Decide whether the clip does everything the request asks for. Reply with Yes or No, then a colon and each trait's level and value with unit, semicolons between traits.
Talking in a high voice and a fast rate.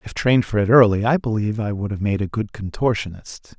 No: low, 105 Hz; fast, 235 wpm